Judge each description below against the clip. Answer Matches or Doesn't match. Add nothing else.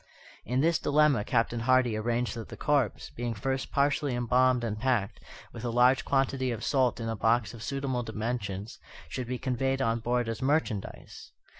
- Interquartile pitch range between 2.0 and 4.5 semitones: Matches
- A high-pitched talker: Doesn't match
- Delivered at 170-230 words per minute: Matches